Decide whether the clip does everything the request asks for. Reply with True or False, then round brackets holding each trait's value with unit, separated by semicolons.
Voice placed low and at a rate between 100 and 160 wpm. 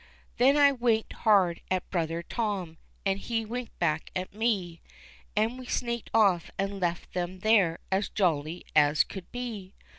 False (195 Hz; 155 wpm)